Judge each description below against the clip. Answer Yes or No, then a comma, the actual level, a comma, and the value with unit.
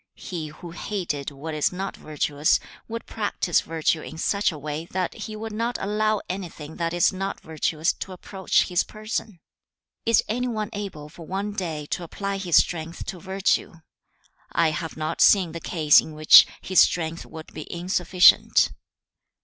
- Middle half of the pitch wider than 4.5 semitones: No, average, 3.9 semitones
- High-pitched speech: No, medium, 175 Hz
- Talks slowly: No, average, 170 wpm